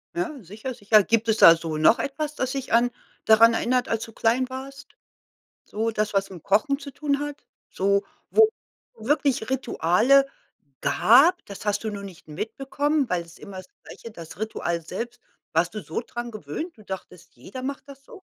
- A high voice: Yes, high, 225 Hz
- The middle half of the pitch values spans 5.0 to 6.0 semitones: Yes, wide, 5.5 semitones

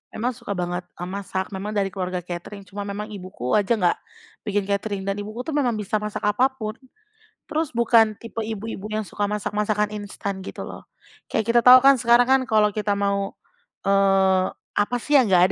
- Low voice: No, high, 205 Hz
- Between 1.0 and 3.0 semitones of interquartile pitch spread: Yes, narrow, 2.4 semitones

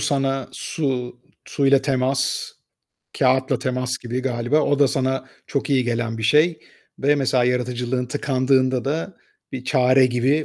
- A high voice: No, low, 130 Hz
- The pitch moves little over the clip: Yes, narrow, 1.7 semitones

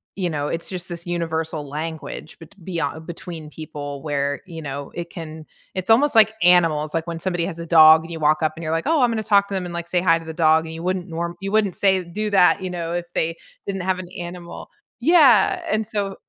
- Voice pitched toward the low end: No, medium, 170 Hz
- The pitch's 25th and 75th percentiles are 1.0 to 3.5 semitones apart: Yes, average, 2.8 semitones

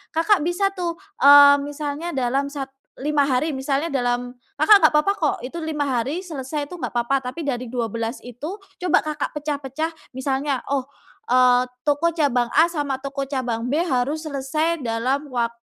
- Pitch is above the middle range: Yes, very high, 280 Hz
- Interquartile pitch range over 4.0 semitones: No, average, 3.6 semitones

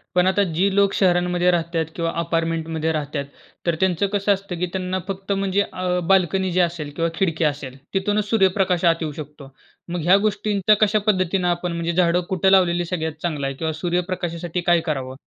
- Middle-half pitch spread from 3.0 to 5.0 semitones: No, narrow, 2.5 semitones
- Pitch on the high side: No, medium, 175 Hz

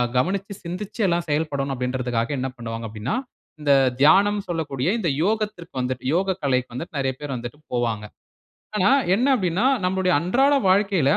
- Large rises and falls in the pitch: Yes, wide, 7.0 semitones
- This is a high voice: No, medium, 155 Hz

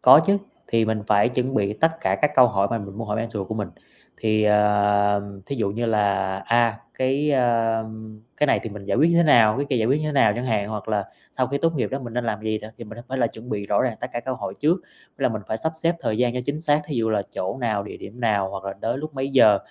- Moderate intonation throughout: Yes, average, 4.0 semitones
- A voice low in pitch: Yes, low, 115 Hz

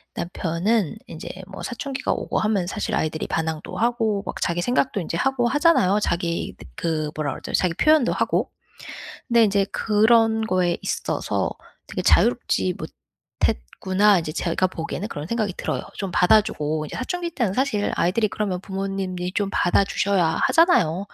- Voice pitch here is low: No, high, 195 Hz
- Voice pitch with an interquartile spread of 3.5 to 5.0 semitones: Yes, average, 4.7 semitones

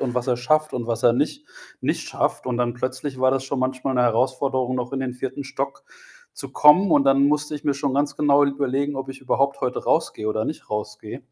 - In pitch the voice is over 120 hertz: Yes, low, 135 Hz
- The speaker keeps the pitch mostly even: Yes, narrow, 2.1 semitones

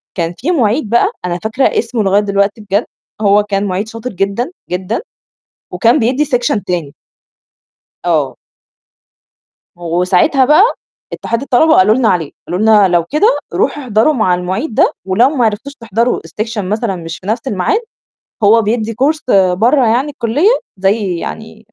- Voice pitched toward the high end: Yes, high, 215 Hz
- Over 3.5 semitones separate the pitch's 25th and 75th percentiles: Yes, average, 4.6 semitones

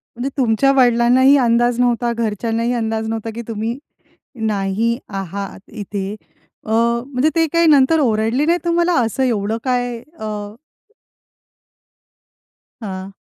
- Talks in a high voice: Yes, high, 235 Hz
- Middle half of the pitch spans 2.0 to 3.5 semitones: Yes, average, 2.7 semitones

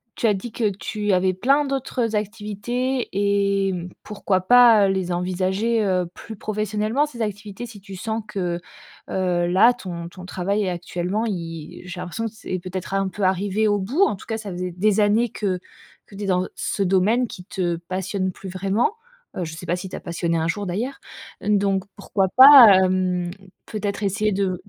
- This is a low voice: No, high, 195 Hz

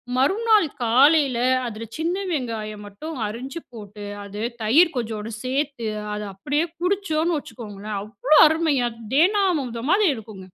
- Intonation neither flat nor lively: No, wide, 6.8 semitones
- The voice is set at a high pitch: Yes, very high, 260 Hz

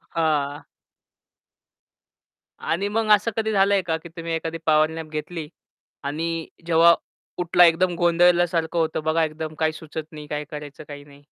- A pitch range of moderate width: No, narrow, 2.0 semitones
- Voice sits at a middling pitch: Yes, medium, 165 Hz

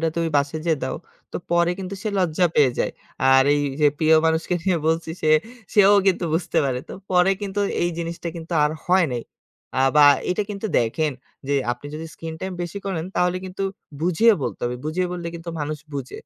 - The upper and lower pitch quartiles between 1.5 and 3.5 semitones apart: Yes, average, 2.9 semitones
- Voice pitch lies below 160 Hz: No, medium, 165 Hz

